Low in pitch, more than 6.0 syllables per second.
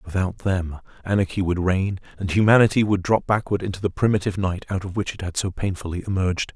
Yes: very low, 95 Hz; 6.2 syllables/s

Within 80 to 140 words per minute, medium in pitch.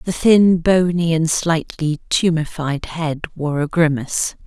Yes: slow, 135 wpm; medium, 160 Hz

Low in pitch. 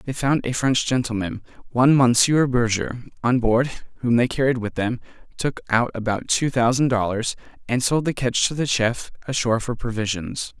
Yes: low, 120 Hz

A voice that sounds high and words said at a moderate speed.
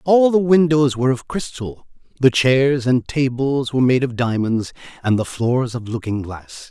No: low, 130 Hz; average, 180 wpm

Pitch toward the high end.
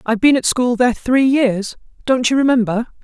Yes: high, 245 Hz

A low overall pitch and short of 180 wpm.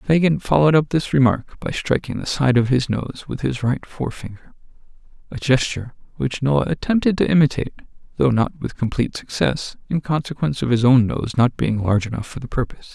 No: low, 130 Hz; average, 185 wpm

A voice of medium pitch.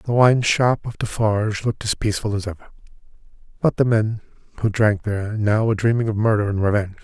No: low, 110 Hz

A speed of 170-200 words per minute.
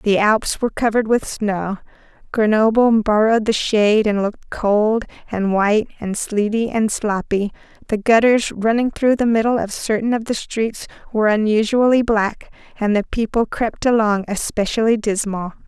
No: average, 155 wpm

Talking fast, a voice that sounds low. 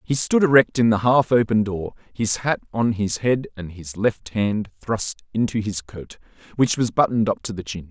Yes: fast, 210 wpm; low, 110 Hz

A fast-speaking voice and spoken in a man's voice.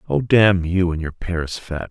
Yes: fast, 220 wpm; male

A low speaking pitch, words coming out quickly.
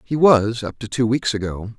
Yes: low, 115 Hz; fast, 235 wpm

